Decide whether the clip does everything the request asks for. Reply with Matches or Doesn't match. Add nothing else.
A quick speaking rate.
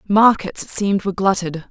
Doesn't match